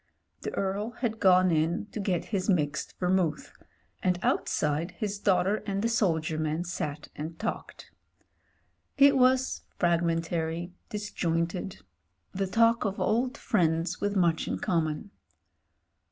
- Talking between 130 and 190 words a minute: Yes, slow, 135 wpm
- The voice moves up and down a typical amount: Yes, average, 4.0 semitones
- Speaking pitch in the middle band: Yes, medium, 180 Hz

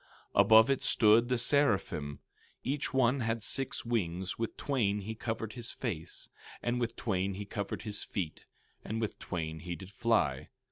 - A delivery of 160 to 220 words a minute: Yes, average, 170 wpm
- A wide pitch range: No, average, 3.9 semitones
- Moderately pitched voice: No, low, 110 Hz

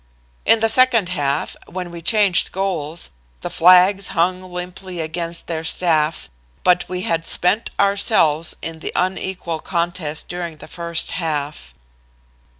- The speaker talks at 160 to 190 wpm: No, slow, 135 wpm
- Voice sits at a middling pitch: Yes, medium, 175 Hz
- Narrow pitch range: Yes, narrow, 2.3 semitones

